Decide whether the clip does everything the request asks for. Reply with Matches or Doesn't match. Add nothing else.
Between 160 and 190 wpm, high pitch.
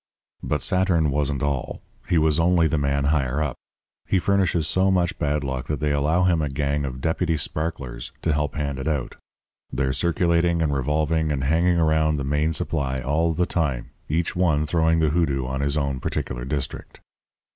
Doesn't match